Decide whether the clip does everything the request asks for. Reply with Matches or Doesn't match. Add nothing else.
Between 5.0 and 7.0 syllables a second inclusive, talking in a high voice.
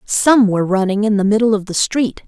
Matches